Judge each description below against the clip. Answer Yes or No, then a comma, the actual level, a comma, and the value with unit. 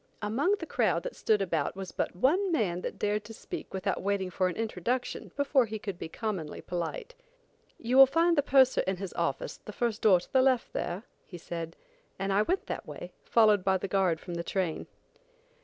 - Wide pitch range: Yes, wide, 6.0 semitones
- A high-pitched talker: Yes, high, 210 Hz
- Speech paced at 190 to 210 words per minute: Yes, fast, 205 wpm